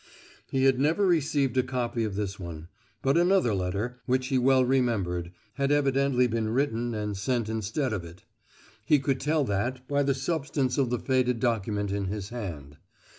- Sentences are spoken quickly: No, average, 175 wpm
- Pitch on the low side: Yes, low, 125 Hz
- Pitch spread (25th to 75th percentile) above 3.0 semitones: Yes, average, 4.6 semitones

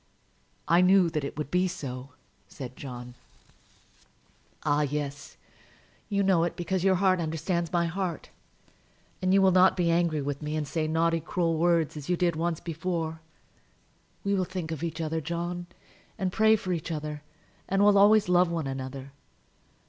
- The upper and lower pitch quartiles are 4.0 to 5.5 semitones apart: No, average, 3.1 semitones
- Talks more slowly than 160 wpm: No, average, 170 wpm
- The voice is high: No, medium, 170 Hz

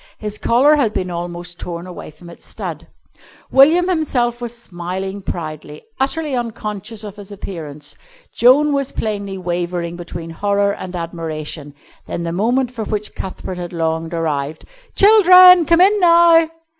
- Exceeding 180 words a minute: No, average, 145 wpm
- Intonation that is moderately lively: No, wide, 7.3 semitones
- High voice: Yes, high, 200 Hz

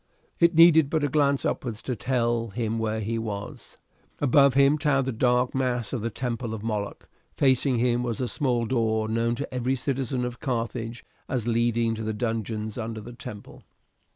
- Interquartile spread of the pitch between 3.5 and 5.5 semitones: No, average, 2.7 semitones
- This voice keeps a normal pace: Yes, average, 180 wpm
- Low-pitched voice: Yes, low, 120 Hz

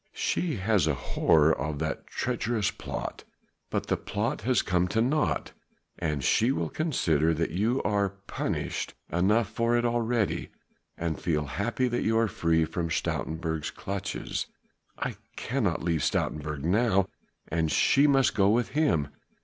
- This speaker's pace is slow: No, average, 150 wpm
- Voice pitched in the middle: No, low, 100 Hz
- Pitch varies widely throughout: Yes, wide, 6.5 semitones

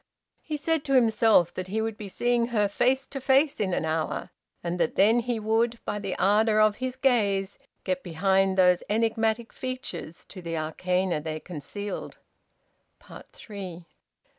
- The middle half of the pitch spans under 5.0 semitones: Yes, average, 4.5 semitones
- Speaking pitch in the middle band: No, high, 210 Hz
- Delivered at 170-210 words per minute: No, average, 160 wpm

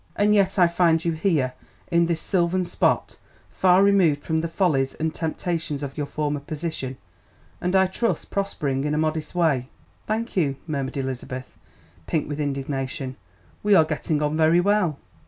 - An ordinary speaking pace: Yes, average, 165 wpm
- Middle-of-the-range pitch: Yes, medium, 160 Hz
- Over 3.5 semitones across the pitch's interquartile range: Yes, average, 3.9 semitones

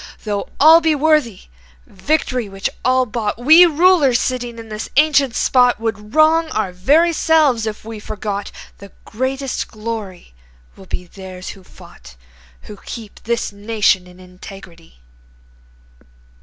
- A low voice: No, high, 225 Hz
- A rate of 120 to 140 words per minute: Yes, slow, 135 wpm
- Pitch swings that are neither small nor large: No, wide, 5.8 semitones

